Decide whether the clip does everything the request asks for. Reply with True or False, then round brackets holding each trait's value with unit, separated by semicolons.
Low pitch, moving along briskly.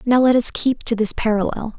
False (230 Hz; 235 wpm)